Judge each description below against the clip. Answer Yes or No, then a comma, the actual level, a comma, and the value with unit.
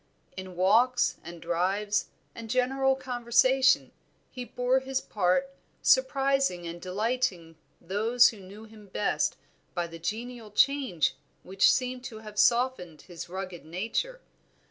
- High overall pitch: Yes, high, 220 Hz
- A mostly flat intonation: No, wide, 5.6 semitones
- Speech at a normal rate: No, slow, 125 wpm